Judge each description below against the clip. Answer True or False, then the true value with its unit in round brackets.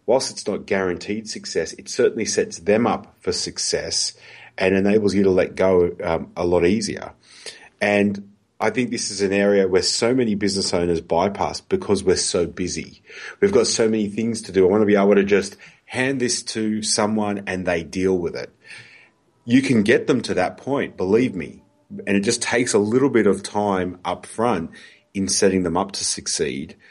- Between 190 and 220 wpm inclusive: True (195 wpm)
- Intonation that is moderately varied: False (2.3 semitones)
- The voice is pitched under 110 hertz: True (100 Hz)